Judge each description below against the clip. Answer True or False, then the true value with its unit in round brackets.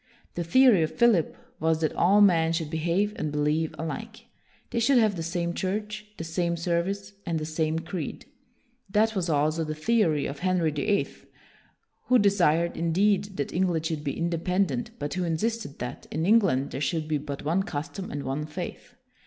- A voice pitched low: False (170 Hz)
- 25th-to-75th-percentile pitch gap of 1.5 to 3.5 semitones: False (4.2 semitones)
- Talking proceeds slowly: False (180 wpm)